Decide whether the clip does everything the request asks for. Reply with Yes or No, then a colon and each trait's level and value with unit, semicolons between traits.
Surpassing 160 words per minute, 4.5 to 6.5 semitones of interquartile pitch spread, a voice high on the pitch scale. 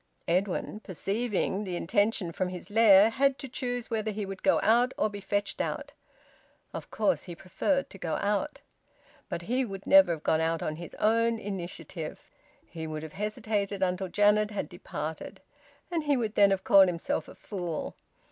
No: average, 175 wpm; average, 3.7 semitones; high, 200 Hz